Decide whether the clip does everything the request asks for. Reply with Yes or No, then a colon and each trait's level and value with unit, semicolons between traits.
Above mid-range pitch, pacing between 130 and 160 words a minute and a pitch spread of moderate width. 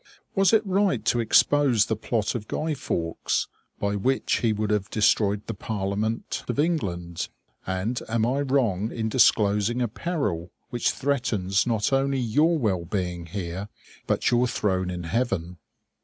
No: low, 110 Hz; average, 155 wpm; average, 4.9 semitones